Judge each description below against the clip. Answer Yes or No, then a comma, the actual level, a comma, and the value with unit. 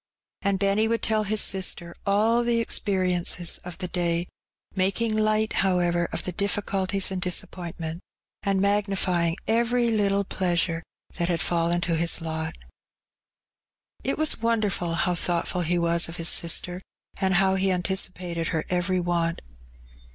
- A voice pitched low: No, medium, 185 Hz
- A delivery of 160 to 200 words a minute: No, average, 145 wpm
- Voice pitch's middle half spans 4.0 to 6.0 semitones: No, average, 2.7 semitones